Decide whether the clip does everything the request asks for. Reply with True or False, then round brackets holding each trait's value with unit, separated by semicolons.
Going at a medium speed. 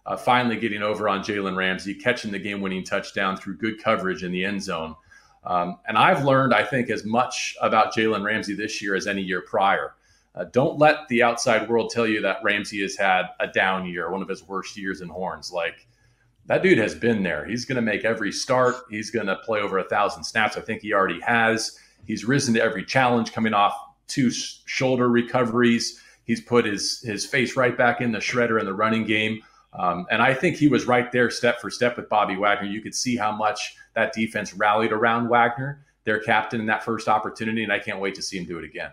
False (225 wpm)